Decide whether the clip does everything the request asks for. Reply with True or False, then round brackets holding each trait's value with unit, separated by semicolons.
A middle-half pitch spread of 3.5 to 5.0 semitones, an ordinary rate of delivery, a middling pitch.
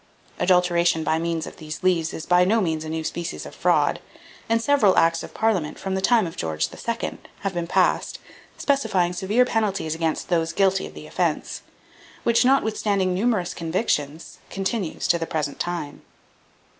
True (4.2 semitones; 170 wpm; 180 Hz)